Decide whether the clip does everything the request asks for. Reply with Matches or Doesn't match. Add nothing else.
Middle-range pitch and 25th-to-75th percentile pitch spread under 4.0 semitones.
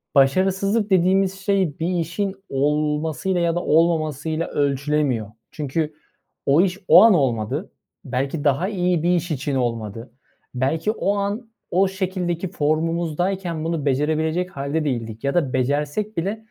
Doesn't match